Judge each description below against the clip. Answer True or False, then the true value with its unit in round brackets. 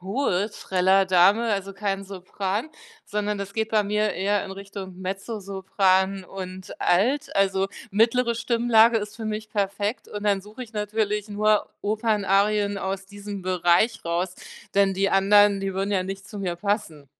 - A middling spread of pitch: False (1.7 semitones)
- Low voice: False (200 Hz)